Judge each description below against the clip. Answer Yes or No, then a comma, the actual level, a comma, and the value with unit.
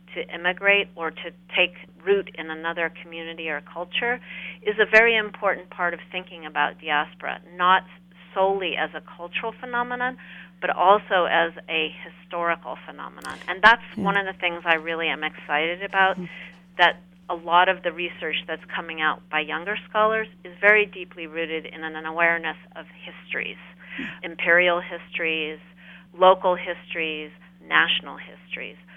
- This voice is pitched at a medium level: Yes, medium, 180 Hz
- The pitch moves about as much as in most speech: No, narrow, 2.2 semitones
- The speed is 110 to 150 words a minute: Yes, average, 145 wpm